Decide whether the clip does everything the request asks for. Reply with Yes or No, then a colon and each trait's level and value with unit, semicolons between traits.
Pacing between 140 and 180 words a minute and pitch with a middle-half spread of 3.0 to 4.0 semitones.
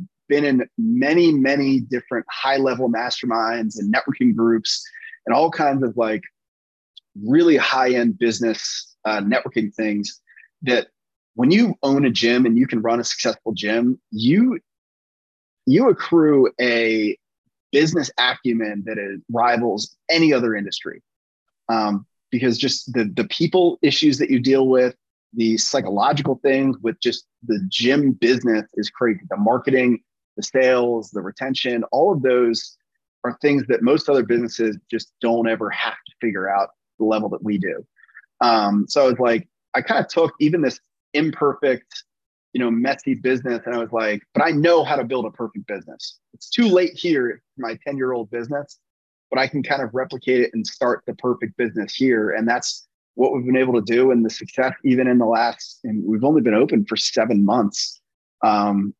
Yes: average, 170 wpm; average, 3.6 semitones